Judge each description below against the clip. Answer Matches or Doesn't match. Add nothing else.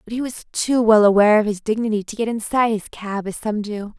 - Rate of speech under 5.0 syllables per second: Doesn't match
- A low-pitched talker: Doesn't match